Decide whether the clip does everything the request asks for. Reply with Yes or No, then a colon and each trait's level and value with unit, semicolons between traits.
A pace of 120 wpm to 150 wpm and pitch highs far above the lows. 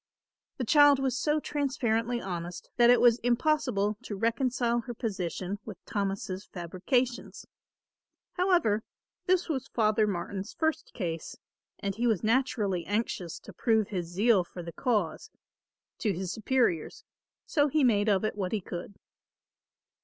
No: average, 140 wpm; average, 4.6 semitones